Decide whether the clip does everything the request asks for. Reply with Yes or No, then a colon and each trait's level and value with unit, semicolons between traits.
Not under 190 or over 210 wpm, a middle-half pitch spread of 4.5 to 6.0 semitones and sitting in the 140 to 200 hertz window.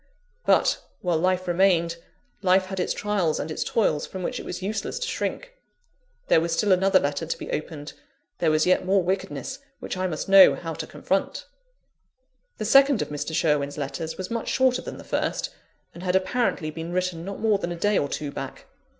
No: average, 200 wpm; average, 3.3 semitones; medium, 185 Hz